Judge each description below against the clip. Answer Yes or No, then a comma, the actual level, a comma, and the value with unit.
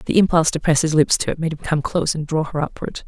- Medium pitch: Yes, medium, 155 Hz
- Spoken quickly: Yes, fast, 310 wpm